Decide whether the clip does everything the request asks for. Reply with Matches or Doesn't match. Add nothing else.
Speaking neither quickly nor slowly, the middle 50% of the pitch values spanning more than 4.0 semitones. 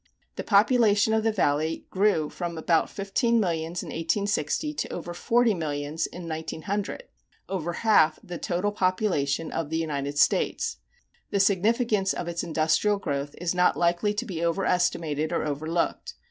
Matches